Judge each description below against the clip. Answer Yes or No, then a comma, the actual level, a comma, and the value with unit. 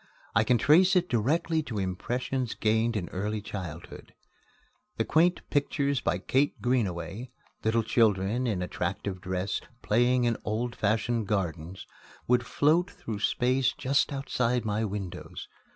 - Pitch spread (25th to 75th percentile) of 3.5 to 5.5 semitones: Yes, average, 4.2 semitones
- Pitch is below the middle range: Yes, low, 115 Hz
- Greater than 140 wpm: No, slow, 135 wpm